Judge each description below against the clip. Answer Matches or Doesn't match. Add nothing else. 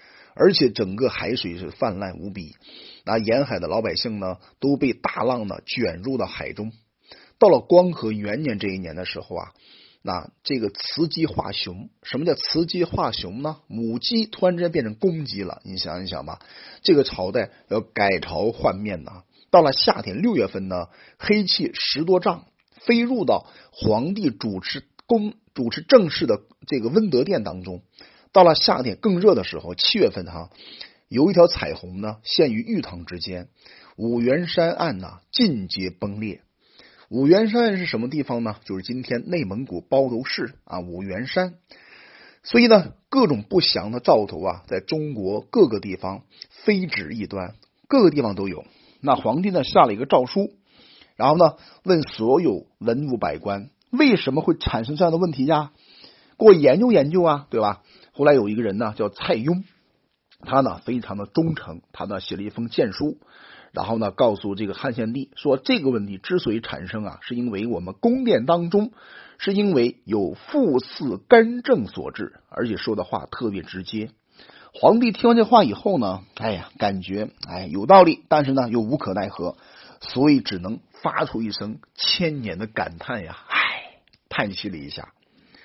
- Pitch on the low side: Matches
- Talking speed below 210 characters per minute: Doesn't match